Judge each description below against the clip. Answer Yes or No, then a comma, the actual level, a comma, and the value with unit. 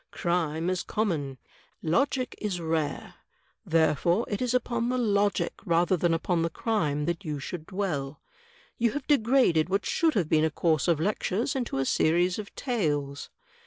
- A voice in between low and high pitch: Yes, medium, 175 Hz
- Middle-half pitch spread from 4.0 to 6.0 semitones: Yes, wide, 5.4 semitones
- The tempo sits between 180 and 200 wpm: No, average, 160 wpm